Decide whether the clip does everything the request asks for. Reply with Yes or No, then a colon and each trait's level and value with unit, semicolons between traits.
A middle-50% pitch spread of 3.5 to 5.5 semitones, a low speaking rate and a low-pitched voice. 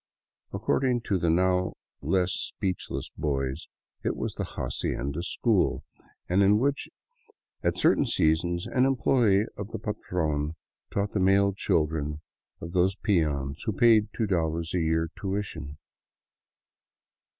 Yes: average, 4.4 semitones; slow, 130 wpm; very low, 90 Hz